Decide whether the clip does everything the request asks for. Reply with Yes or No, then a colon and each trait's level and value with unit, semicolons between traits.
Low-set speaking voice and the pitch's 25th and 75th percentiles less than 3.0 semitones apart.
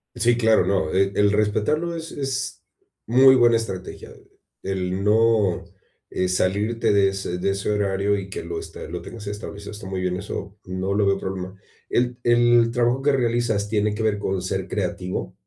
No: low, 105 Hz; average, 3.5 semitones